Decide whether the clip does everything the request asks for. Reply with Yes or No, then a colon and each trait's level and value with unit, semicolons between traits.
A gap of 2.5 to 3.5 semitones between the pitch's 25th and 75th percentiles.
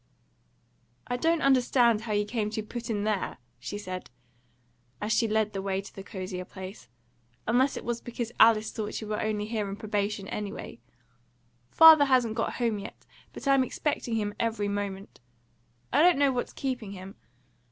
Yes: average, 3.0 semitones